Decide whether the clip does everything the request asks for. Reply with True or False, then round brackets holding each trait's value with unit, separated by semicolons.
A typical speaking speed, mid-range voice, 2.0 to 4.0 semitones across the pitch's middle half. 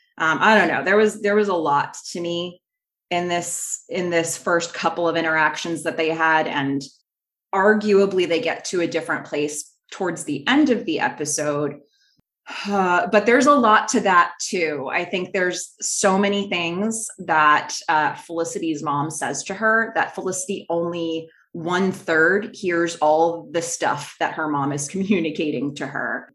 True (170 wpm; 170 Hz; 3.4 semitones)